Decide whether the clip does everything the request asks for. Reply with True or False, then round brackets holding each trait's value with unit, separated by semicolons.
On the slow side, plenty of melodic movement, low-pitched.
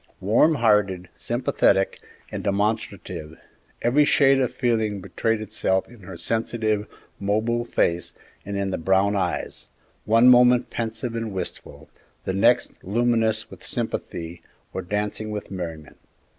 False (130 wpm; 3.5 semitones; 105 Hz)